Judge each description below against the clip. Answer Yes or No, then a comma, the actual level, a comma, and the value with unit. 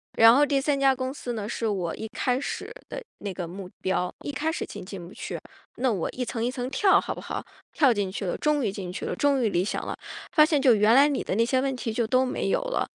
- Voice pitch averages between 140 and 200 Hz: No, high, 245 Hz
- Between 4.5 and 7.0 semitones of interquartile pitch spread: Yes, average, 5.3 semitones